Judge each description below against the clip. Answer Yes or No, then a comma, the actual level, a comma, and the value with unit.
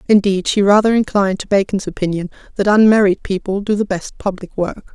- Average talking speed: Yes, average, 180 wpm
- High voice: Yes, high, 200 Hz